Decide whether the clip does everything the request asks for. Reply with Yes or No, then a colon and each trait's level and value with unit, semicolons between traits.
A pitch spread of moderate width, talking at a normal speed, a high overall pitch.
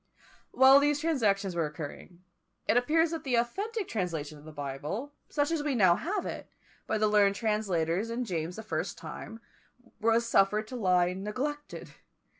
No: wide, 7.4 semitones; average, 165 wpm; high, 215 Hz